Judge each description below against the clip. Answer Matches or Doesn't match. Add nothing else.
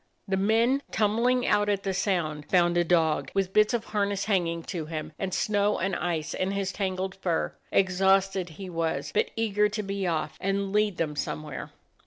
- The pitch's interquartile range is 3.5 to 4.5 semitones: Doesn't match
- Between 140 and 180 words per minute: Doesn't match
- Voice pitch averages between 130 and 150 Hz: Doesn't match